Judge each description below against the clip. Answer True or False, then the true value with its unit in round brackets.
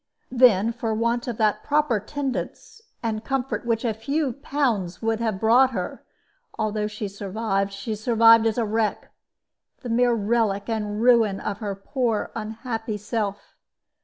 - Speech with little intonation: True (2.3 semitones)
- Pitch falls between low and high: False (225 Hz)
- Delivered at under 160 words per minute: True (150 wpm)